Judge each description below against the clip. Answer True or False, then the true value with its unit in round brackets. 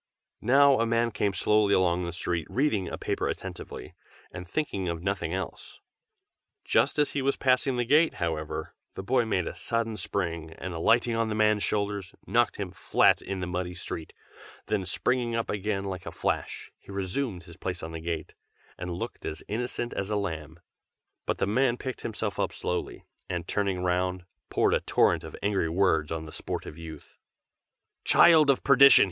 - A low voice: True (100 Hz)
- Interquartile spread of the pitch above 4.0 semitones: True (5.0 semitones)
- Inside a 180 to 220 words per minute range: True (185 wpm)